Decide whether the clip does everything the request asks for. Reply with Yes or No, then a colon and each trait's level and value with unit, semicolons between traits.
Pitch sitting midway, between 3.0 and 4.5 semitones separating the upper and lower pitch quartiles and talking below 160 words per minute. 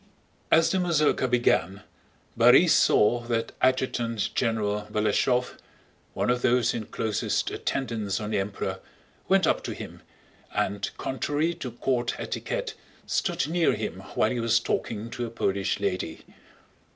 No: low, 115 Hz; average, 3.4 semitones; average, 140 wpm